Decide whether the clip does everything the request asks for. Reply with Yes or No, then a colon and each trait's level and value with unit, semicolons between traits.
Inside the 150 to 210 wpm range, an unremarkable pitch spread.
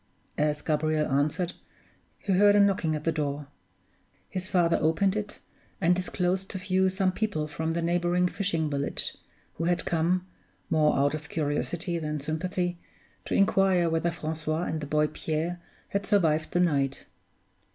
Yes: average, 155 wpm; average, 3.1 semitones